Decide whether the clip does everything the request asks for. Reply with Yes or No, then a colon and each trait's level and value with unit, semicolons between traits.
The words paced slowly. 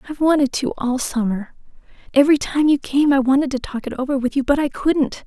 No: fast, 205 wpm